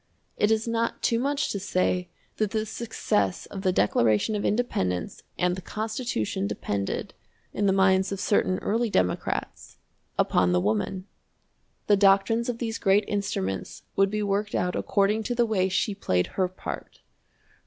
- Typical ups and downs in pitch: Yes, average, 3.5 semitones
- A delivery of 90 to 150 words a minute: No, average, 160 wpm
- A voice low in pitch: No, high, 195 Hz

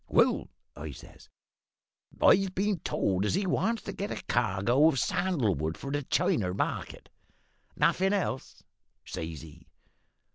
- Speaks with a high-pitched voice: No, low, 135 Hz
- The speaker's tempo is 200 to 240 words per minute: No, average, 140 wpm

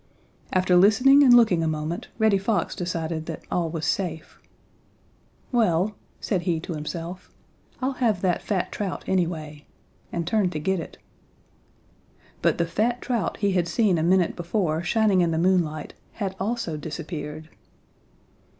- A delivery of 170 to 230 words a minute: No, average, 150 wpm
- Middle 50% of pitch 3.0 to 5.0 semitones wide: Yes, average, 4.0 semitones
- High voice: No, medium, 180 Hz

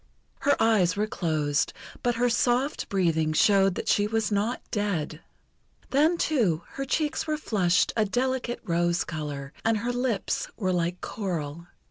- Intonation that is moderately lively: No, wide, 6.1 semitones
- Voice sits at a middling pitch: No, high, 205 Hz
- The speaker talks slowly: No, average, 150 wpm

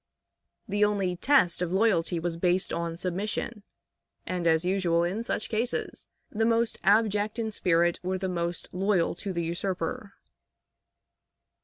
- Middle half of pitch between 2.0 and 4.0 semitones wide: Yes, average, 3.4 semitones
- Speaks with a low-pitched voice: No, medium, 185 Hz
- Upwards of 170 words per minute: No, average, 140 wpm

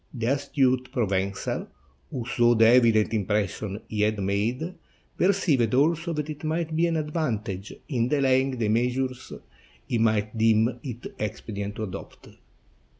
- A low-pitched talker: Yes, low, 120 Hz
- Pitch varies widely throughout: No, average, 4.6 semitones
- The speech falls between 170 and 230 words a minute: No, average, 145 wpm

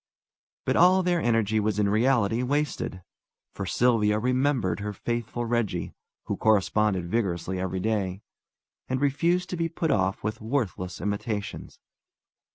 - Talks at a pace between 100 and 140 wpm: Yes, slow, 135 wpm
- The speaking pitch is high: No, low, 110 Hz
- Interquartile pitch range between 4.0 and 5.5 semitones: Yes, average, 4.3 semitones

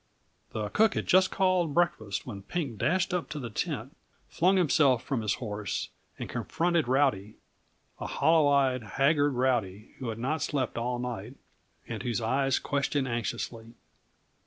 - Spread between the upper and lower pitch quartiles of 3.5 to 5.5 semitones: Yes, average, 5.1 semitones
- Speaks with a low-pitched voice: Yes, low, 130 Hz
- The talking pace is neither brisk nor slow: Yes, average, 155 wpm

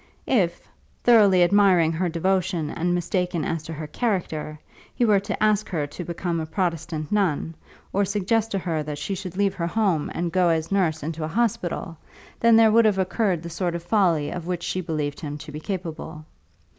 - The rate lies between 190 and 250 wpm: Yes, average, 195 wpm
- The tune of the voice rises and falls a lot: No, average, 3.5 semitones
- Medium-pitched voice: Yes, medium, 175 Hz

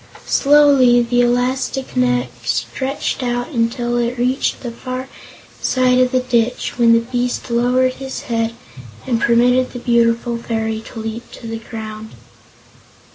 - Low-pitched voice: No, high, 240 Hz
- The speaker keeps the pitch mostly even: Yes, narrow, 1.8 semitones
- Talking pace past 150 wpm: No, average, 140 wpm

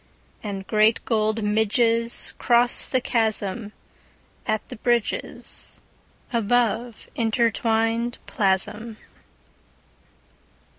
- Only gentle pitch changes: Yes, narrow, 1.8 semitones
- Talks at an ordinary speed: No, slow, 55 wpm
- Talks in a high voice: Yes, high, 225 Hz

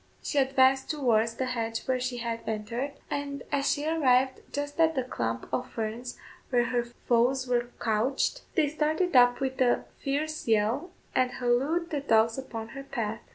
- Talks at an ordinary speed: Yes, average, 170 wpm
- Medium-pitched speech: No, very high, 255 Hz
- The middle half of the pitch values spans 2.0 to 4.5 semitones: Yes, average, 3.2 semitones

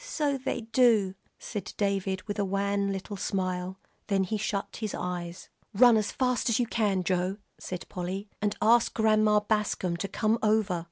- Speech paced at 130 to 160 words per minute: No, average, 170 wpm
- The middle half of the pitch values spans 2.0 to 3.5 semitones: Yes, narrow, 2.5 semitones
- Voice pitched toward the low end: No, high, 205 Hz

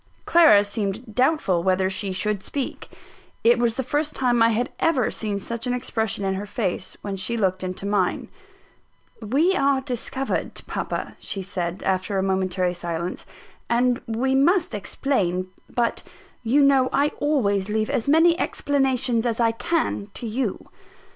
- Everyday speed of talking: Yes, average, 155 wpm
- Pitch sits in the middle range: No, high, 225 Hz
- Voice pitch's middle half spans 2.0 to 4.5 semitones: No, wide, 5.4 semitones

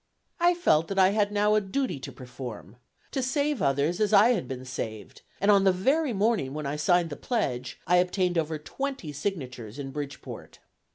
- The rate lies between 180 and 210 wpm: Yes, average, 190 wpm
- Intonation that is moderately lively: No, wide, 7.4 semitones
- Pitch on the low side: No, medium, 180 Hz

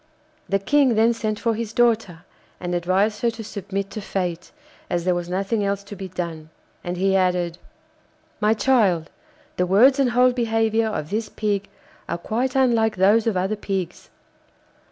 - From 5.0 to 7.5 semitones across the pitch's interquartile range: No, average, 3.7 semitones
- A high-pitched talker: Yes, high, 205 Hz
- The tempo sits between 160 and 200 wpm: Yes, average, 170 wpm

